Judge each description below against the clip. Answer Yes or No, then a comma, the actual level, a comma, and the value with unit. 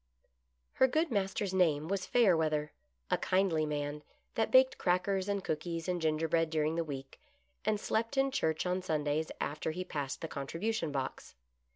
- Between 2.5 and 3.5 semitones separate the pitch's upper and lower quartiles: No, average, 4.3 semitones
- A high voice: No, medium, 165 Hz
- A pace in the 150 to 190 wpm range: Yes, average, 160 wpm